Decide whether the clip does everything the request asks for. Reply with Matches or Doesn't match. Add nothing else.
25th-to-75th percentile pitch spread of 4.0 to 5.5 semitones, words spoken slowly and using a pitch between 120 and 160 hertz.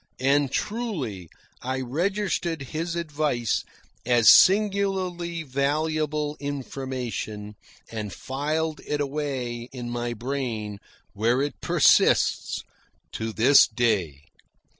Matches